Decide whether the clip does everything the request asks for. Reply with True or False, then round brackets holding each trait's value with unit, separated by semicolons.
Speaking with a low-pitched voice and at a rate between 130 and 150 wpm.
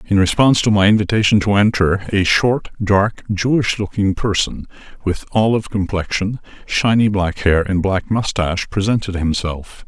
True (100 Hz; 145 wpm)